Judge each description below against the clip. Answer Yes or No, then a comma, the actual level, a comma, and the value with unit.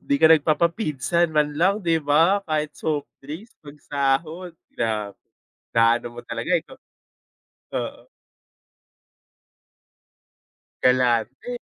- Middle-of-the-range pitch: Yes, medium, 150 Hz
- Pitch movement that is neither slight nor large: Yes, average, 4.0 semitones